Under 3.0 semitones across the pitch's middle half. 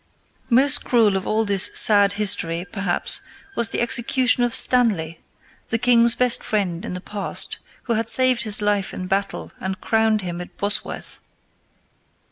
No: average, 3.6 semitones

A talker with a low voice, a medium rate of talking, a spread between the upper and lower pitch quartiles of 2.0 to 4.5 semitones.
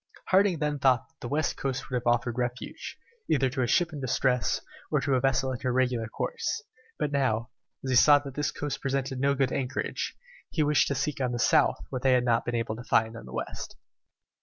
No: low, 130 Hz; fast, 230 wpm; narrow, 2.4 semitones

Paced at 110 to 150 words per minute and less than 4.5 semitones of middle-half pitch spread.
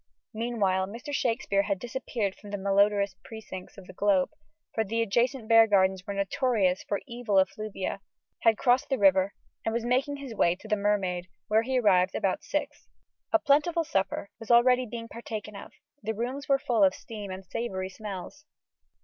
No: average, 175 wpm; average, 3.7 semitones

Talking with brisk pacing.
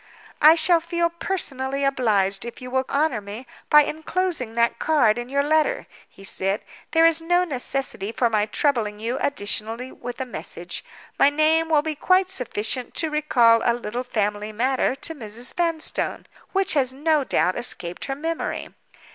No: average, 165 wpm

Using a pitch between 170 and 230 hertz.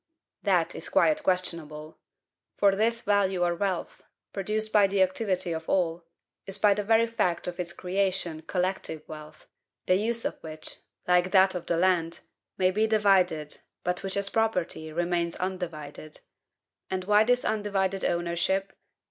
Yes: medium, 185 Hz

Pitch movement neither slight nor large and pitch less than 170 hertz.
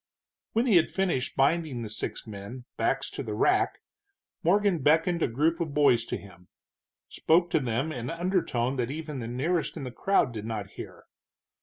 No: wide, 6.2 semitones; medium, 140 Hz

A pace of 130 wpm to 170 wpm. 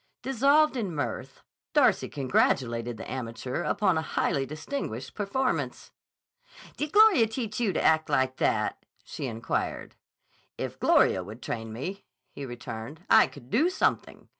Yes: average, 140 wpm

